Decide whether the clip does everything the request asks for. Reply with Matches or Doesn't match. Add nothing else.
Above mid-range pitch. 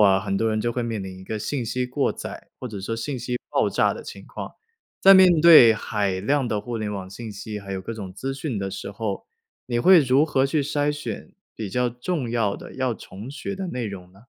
Doesn't match